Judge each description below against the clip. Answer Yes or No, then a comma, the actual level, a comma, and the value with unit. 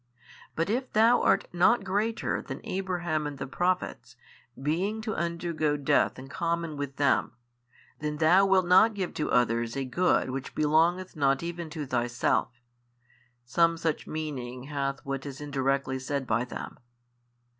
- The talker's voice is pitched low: No, medium, 155 Hz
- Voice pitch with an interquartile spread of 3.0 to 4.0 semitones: No, average, 4.6 semitones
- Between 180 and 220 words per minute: No, average, 150 wpm